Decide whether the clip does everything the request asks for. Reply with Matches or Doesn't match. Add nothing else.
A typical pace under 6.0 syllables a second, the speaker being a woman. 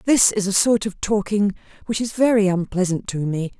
Matches